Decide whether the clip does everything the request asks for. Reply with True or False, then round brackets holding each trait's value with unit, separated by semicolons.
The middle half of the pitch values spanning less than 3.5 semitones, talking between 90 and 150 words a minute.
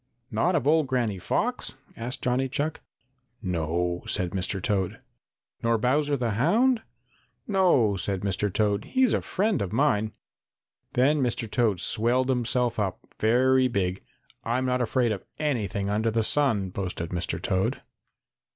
False (4.8 semitones; 140 wpm)